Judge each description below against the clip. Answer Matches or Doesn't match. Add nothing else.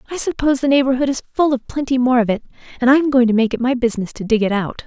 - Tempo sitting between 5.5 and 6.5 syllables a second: Doesn't match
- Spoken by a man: Doesn't match